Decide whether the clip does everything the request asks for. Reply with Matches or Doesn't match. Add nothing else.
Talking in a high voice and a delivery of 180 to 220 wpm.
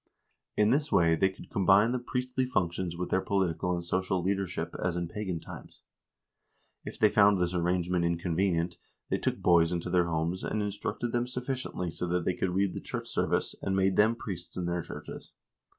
Doesn't match